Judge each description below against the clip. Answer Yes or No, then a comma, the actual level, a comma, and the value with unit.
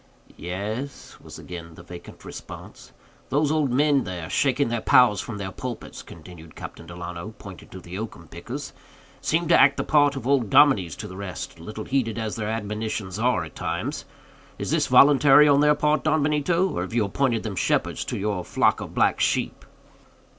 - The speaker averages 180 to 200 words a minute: Yes, average, 185 wpm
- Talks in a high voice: No, low, 110 Hz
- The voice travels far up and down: Yes, wide, 7.3 semitones